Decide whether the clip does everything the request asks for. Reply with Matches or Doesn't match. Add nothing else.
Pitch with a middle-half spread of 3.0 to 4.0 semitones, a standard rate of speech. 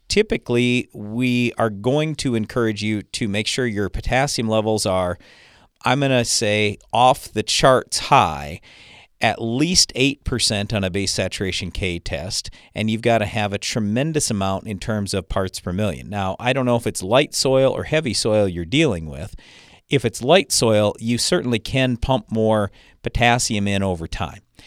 Matches